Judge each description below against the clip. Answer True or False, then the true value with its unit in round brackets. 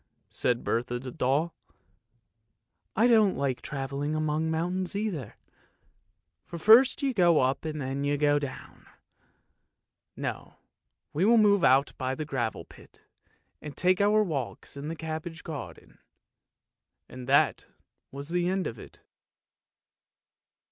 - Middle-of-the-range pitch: True (150 Hz)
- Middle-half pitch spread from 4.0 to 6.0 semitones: True (5.2 semitones)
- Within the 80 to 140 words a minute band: True (135 wpm)